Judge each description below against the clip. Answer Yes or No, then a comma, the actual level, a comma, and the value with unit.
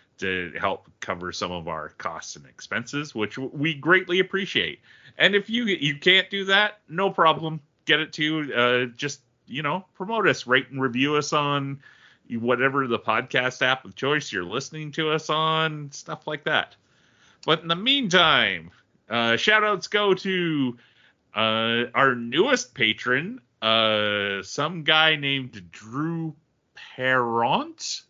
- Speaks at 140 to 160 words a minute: Yes, average, 145 wpm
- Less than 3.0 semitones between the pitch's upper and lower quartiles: No, wide, 5.6 semitones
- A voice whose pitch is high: No, medium, 140 Hz